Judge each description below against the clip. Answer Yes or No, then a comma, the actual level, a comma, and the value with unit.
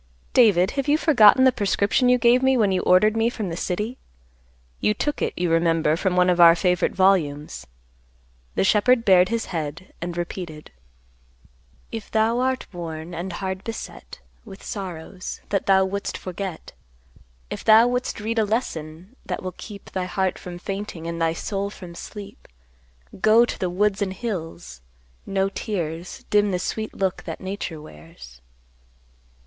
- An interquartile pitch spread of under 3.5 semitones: No, average, 3.9 semitones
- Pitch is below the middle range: No, high, 190 Hz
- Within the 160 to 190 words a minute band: Yes, average, 165 wpm